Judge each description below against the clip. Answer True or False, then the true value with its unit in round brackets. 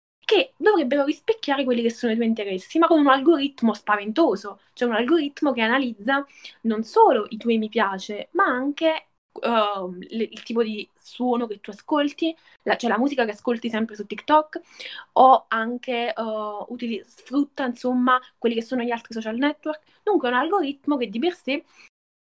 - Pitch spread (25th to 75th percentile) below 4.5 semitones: False (4.8 semitones)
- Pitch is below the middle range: False (245 Hz)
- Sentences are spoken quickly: True (180 wpm)